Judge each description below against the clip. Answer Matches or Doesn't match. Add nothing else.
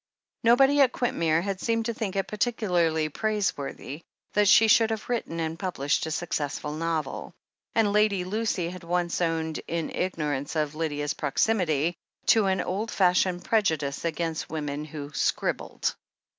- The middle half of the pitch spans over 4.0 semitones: Matches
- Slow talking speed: Doesn't match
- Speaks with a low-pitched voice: Doesn't match